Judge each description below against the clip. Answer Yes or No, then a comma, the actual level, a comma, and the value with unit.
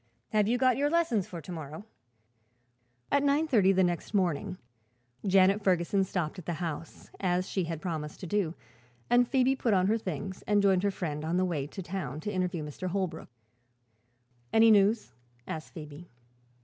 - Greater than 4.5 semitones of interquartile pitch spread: No, average, 3.8 semitones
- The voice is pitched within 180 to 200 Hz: Yes, medium, 185 Hz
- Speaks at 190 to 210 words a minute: No, average, 175 wpm